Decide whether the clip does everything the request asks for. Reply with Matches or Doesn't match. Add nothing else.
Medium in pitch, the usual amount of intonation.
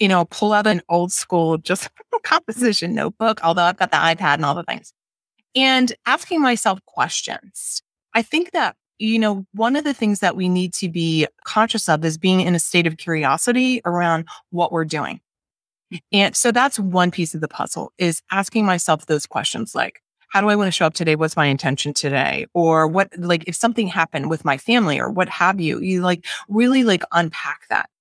Matches